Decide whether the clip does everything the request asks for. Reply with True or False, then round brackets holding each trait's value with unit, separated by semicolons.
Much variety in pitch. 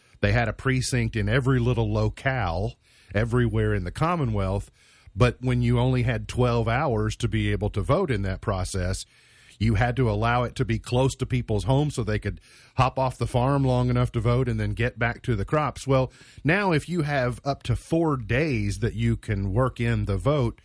False (3.3 semitones)